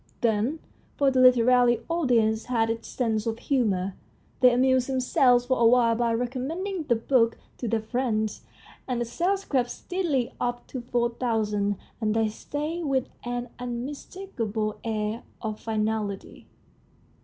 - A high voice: Yes, high, 240 Hz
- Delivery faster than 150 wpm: No, average, 145 wpm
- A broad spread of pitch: No, narrow, 2.6 semitones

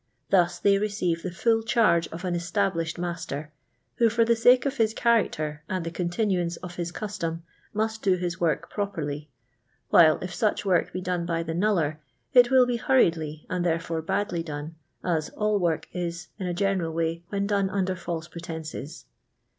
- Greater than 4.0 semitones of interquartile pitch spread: No, average, 3.6 semitones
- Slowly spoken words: No, average, 180 wpm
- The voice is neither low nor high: Yes, medium, 175 Hz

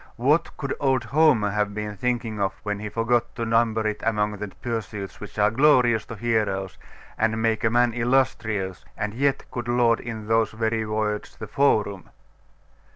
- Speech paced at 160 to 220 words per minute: Yes, average, 165 wpm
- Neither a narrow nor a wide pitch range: No, narrow, 2.3 semitones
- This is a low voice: Yes, low, 110 Hz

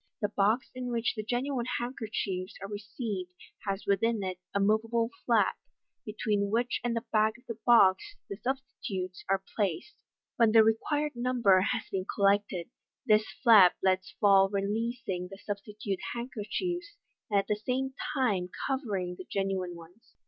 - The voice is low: No, high, 215 Hz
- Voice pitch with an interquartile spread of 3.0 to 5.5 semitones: Yes, average, 3.6 semitones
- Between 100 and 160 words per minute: Yes, average, 155 wpm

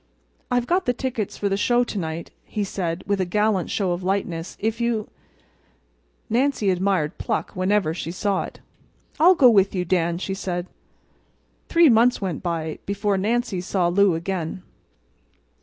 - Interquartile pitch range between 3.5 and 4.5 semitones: Yes, average, 3.9 semitones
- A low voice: No, high, 195 Hz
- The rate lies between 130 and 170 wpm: Yes, average, 160 wpm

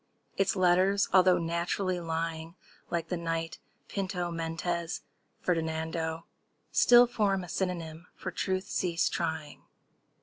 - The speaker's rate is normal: No, slow, 100 wpm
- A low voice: No, medium, 170 Hz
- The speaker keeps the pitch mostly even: Yes, narrow, 2.2 semitones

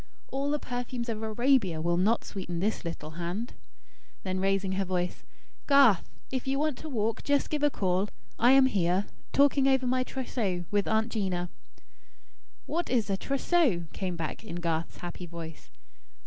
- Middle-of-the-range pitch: No, high, 210 Hz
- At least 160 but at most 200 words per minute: Yes, average, 165 wpm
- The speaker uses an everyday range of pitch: No, wide, 6.6 semitones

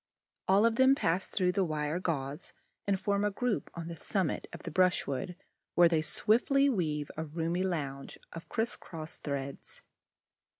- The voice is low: No, medium, 175 Hz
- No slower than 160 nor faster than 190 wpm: Yes, average, 165 wpm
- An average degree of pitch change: Yes, average, 4.4 semitones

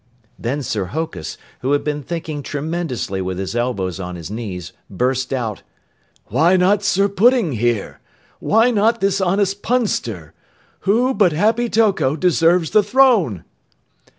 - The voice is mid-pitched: Yes, medium, 160 Hz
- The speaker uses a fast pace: No, average, 140 wpm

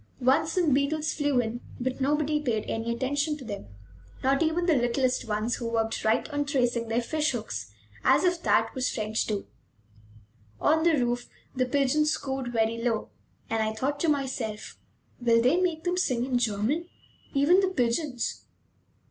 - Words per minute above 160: Yes, average, 170 wpm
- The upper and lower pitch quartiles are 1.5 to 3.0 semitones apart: No, average, 4.5 semitones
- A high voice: Yes, very high, 260 Hz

